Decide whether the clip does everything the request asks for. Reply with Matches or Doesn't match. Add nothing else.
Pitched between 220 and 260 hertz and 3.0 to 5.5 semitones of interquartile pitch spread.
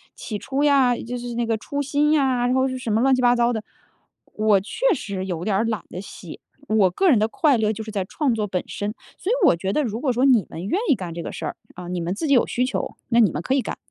Matches